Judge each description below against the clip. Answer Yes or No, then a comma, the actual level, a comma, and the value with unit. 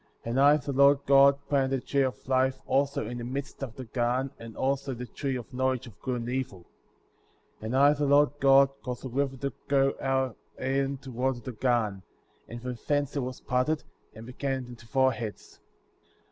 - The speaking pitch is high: No, low, 130 Hz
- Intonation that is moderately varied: No, narrow, 2.0 semitones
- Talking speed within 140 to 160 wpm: No, fast, 205 wpm